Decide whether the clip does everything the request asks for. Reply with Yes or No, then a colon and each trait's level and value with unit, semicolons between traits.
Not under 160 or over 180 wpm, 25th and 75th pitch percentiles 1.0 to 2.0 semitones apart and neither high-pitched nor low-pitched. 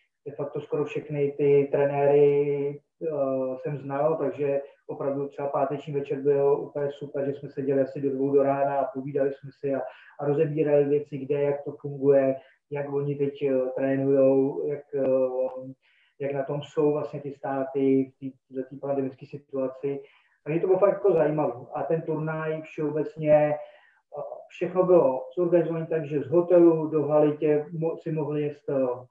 Yes: average, 165 wpm; narrow, 1.5 semitones; medium, 145 Hz